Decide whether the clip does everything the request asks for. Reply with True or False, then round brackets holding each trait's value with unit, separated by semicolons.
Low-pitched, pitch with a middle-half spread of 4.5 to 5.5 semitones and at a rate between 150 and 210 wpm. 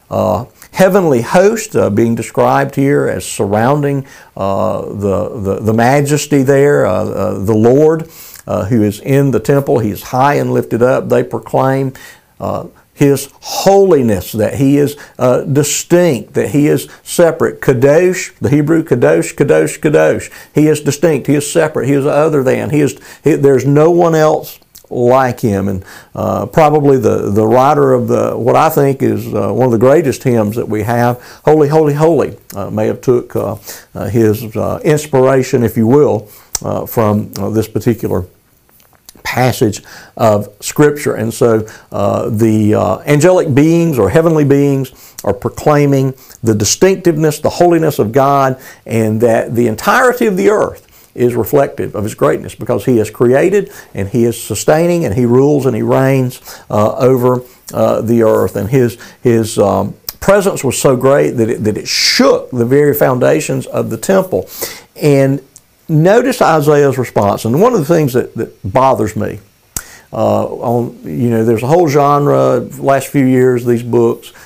True (130 Hz; 4.9 semitones; 170 wpm)